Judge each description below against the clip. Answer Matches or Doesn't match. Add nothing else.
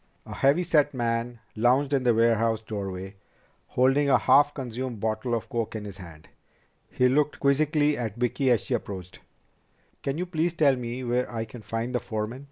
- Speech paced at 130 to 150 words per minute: Doesn't match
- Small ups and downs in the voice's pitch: Doesn't match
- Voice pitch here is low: Matches